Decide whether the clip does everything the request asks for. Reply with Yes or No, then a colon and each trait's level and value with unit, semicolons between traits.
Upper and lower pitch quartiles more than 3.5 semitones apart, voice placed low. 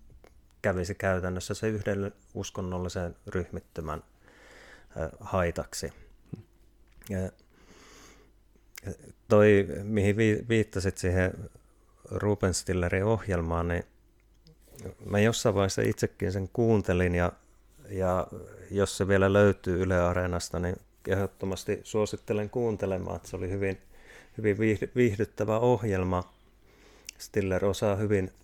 No: narrow, 2.4 semitones; low, 100 Hz